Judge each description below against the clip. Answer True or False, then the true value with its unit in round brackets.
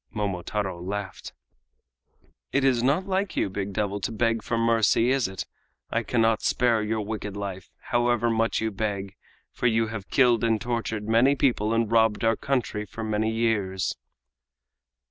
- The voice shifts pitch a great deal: False (2.4 semitones)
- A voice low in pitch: True (110 Hz)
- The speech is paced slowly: False (160 wpm)